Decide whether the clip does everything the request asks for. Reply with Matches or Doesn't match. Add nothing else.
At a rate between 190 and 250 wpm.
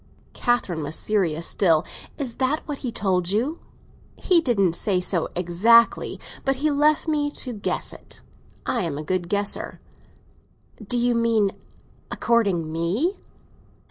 Doesn't match